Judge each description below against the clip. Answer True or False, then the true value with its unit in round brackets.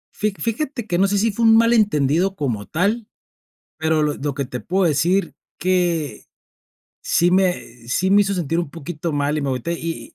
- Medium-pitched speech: True (175 Hz)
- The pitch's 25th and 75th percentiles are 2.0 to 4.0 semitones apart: False (5.0 semitones)